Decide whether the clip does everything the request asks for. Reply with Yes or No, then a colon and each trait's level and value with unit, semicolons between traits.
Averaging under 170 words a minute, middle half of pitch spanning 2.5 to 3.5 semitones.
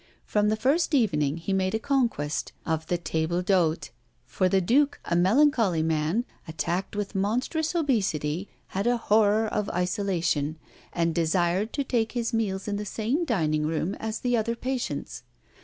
No: average, 160 wpm; wide, 5.6 semitones